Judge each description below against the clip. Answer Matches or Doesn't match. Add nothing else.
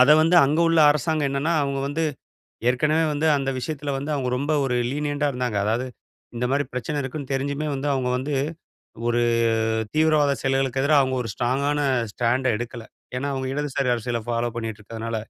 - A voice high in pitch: Doesn't match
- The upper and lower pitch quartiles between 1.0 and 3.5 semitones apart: Matches